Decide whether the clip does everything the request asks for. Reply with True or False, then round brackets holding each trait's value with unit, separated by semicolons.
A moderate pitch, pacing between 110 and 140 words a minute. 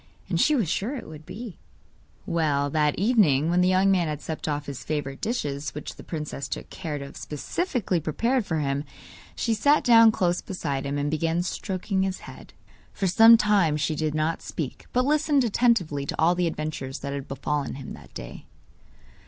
False (165 Hz; 195 wpm)